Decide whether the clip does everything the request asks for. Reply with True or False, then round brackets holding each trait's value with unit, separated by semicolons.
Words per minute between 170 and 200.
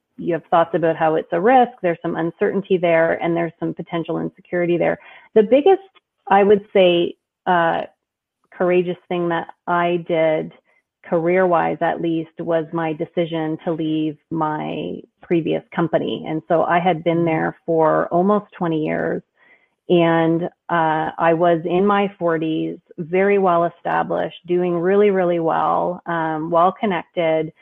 False (150 wpm)